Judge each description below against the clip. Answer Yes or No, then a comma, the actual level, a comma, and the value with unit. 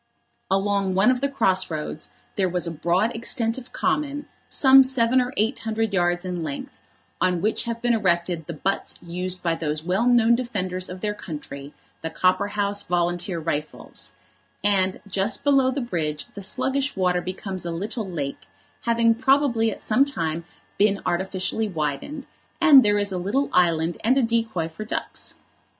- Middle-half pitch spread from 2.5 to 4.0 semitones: No, average, 5.0 semitones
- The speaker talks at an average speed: Yes, average, 165 wpm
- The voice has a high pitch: Yes, high, 195 Hz